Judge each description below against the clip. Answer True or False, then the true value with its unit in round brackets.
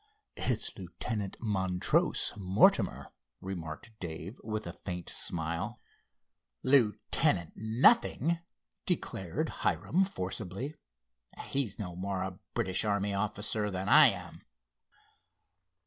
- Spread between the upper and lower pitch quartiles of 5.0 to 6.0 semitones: False (3.3 semitones)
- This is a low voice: True (100 Hz)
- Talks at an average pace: False (95 wpm)